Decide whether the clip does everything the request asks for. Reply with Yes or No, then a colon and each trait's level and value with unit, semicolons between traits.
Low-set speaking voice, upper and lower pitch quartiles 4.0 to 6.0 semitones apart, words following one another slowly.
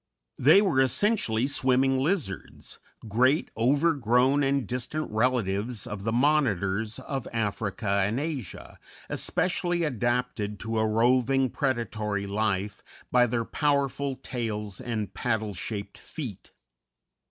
Yes: low, 120 Hz; average, 4.4 semitones; slow, 110 wpm